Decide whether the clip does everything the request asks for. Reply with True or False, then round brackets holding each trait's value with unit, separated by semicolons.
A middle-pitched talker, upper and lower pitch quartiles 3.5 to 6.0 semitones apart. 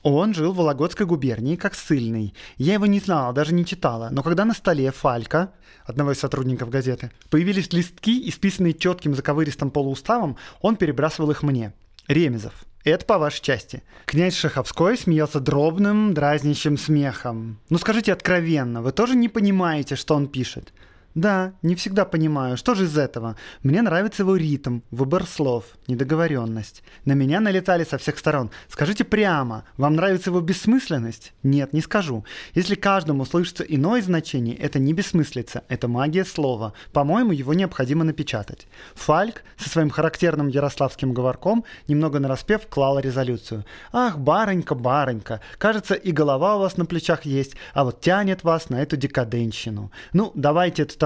True (150 Hz; 5.3 semitones)